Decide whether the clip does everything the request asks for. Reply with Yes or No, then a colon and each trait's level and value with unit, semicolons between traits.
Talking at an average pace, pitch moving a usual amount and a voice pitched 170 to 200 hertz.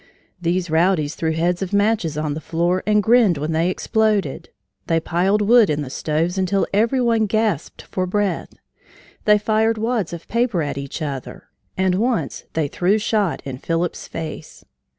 Yes: average, 170 wpm; average, 4.8 semitones; medium, 185 Hz